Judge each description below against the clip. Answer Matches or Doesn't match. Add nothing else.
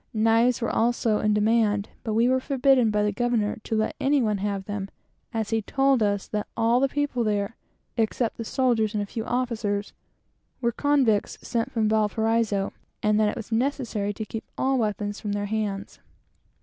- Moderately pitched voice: Doesn't match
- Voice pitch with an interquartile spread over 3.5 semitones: Doesn't match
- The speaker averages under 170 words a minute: Doesn't match